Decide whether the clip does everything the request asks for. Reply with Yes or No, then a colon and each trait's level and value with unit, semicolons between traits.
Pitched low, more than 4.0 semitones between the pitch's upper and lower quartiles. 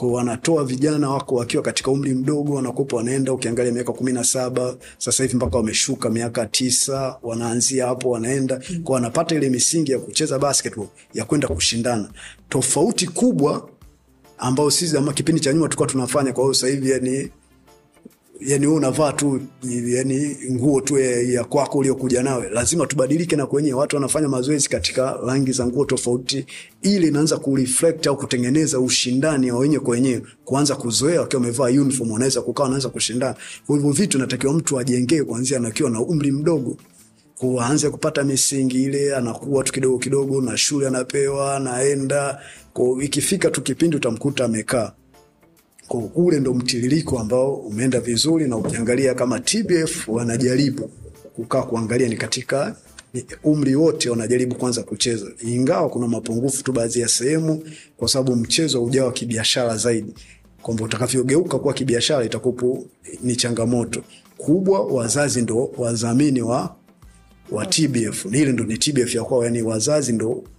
No: low, 130 Hz; average, 2.7 semitones